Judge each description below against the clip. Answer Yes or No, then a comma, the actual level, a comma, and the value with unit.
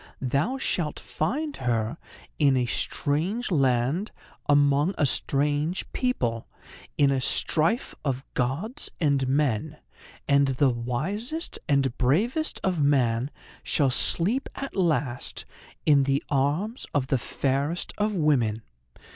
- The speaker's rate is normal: No, slow, 120 wpm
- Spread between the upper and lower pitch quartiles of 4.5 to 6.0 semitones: Yes, wide, 5.4 semitones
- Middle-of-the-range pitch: Yes, medium, 145 Hz